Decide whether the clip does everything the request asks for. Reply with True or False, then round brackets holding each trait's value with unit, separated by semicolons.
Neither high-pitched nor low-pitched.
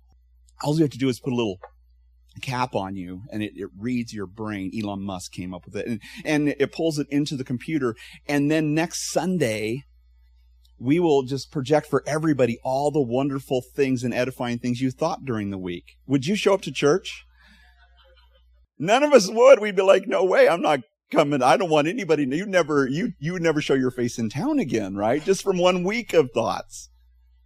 False (130 Hz)